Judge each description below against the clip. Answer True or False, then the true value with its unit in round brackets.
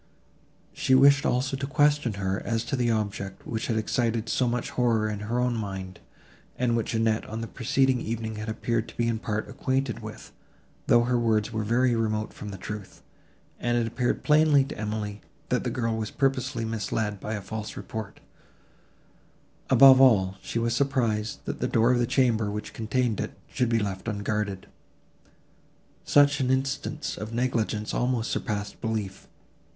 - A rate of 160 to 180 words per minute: True (175 wpm)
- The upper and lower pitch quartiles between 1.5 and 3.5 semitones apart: True (2.8 semitones)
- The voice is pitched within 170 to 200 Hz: False (115 Hz)